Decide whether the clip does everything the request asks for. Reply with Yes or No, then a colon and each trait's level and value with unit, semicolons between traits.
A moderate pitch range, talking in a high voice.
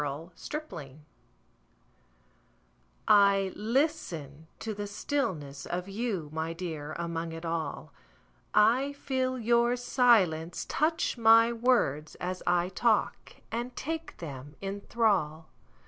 No: wide, 6.8 semitones; high, 195 Hz